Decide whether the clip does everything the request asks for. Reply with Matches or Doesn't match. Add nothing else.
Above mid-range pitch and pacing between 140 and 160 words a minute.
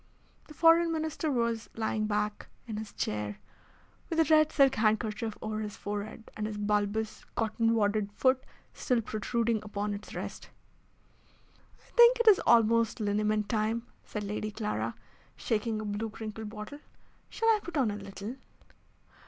Matches